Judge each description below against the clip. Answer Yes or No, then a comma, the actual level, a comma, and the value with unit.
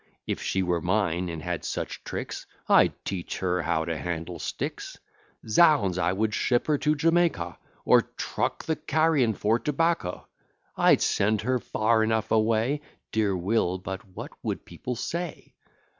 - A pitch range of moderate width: No, wide, 6.2 semitones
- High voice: No, low, 110 Hz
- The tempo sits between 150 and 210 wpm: Yes, average, 160 wpm